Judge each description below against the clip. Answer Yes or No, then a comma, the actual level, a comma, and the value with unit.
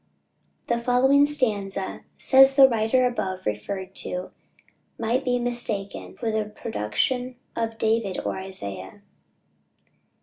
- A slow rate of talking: Yes, slow, 110 wpm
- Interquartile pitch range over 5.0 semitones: No, average, 4.5 semitones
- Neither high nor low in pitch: No, high, 225 Hz